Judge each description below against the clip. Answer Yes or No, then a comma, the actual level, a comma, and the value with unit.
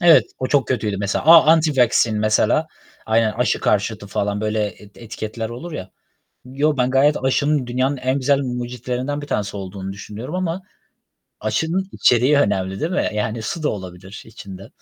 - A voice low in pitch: Yes, low, 120 Hz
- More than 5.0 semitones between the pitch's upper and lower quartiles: Yes, wide, 5.4 semitones